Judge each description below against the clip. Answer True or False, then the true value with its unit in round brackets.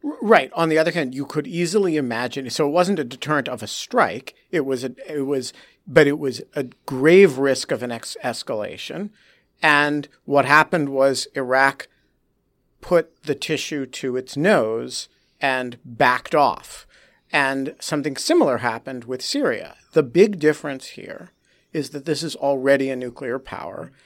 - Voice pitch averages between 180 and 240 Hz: False (140 Hz)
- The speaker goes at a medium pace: True (160 wpm)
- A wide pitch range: False (3.1 semitones)